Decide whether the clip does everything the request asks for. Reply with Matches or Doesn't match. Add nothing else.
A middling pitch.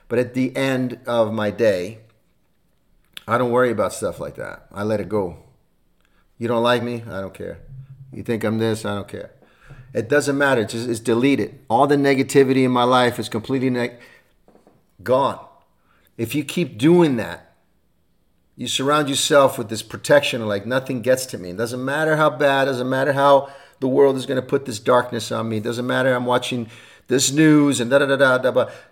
Doesn't match